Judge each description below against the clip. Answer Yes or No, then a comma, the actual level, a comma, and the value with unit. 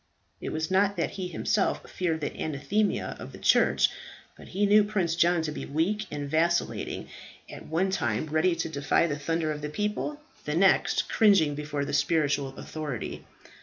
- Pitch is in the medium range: Yes, medium, 160 Hz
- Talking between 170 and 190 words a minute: Yes, average, 175 wpm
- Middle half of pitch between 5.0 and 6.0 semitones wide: No, average, 4.4 semitones